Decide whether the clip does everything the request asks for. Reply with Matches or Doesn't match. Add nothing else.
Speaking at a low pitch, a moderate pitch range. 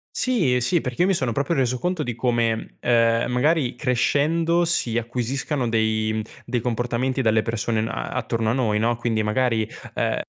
Matches